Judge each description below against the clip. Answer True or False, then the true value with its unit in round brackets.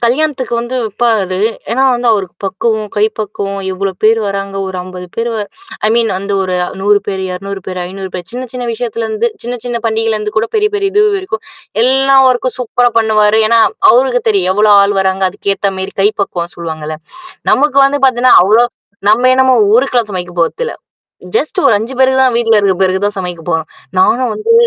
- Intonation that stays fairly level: False (4.2 semitones)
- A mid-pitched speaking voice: False (220 Hz)